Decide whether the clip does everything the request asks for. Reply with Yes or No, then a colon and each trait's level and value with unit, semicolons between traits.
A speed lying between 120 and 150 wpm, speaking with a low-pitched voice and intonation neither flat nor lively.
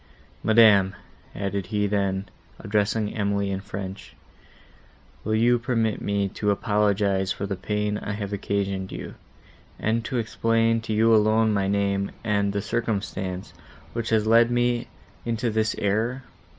No: average, 140 wpm; low, 105 Hz; narrow, 2.2 semitones